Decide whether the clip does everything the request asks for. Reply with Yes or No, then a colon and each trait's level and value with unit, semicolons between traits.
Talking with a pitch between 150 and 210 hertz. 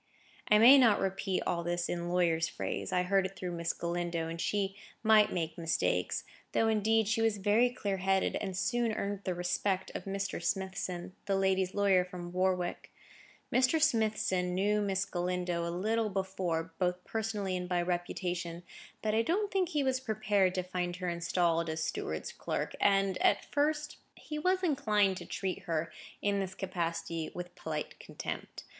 Yes: high, 190 Hz